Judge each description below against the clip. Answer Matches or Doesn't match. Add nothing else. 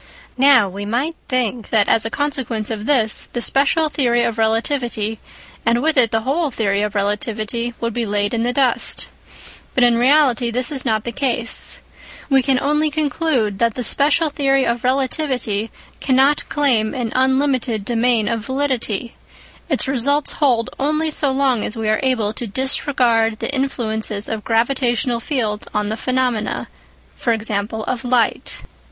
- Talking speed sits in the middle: Matches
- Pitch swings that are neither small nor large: Matches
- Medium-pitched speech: Doesn't match